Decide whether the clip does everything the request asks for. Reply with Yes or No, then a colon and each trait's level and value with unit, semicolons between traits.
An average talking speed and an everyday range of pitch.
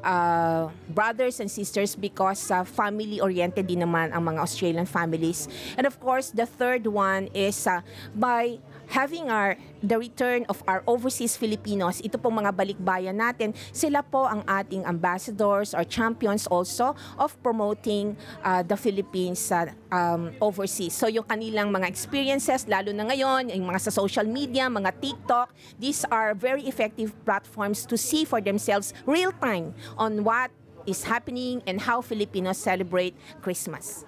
Yes: average, 150 wpm; average, 4.3 semitones